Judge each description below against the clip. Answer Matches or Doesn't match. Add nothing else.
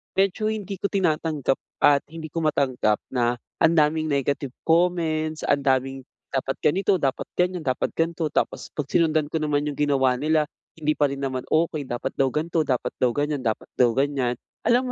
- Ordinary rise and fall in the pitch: Matches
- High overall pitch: Doesn't match